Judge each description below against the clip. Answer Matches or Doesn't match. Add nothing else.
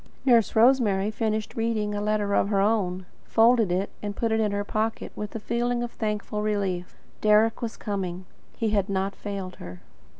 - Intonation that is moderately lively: Doesn't match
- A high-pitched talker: Matches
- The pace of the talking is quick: Doesn't match